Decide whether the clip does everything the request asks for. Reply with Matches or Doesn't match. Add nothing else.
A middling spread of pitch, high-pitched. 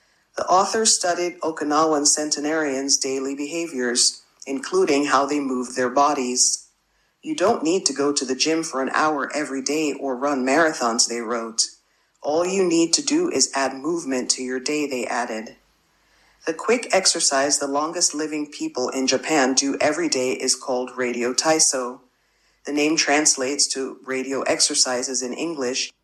Doesn't match